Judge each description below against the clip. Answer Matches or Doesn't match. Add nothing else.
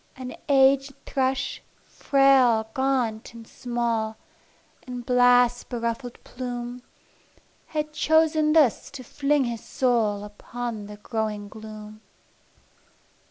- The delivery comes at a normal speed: Doesn't match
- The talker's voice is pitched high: Matches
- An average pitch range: Matches